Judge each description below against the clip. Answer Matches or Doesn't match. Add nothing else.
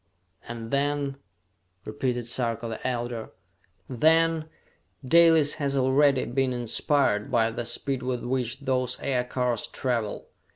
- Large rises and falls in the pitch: Doesn't match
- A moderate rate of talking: Doesn't match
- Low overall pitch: Matches